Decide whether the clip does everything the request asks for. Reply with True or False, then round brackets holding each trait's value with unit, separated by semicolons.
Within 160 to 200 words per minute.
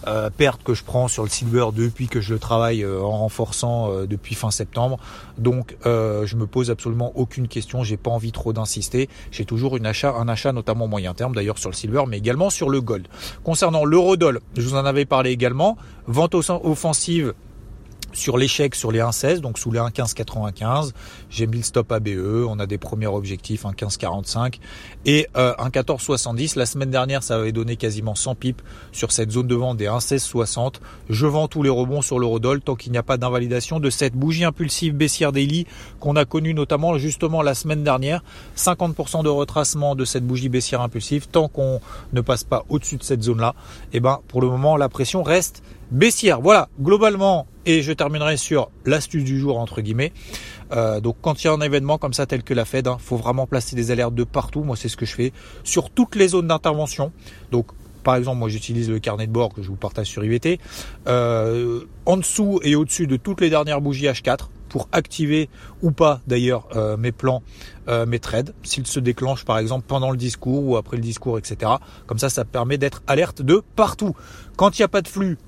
False (210 wpm)